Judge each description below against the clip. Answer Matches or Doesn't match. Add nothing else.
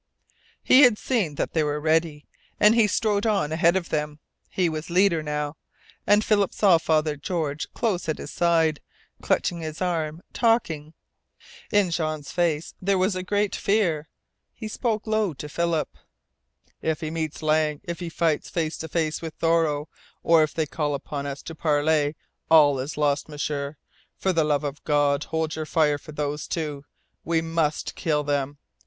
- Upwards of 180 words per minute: Doesn't match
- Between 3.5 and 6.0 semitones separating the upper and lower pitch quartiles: Doesn't match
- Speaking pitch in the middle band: Matches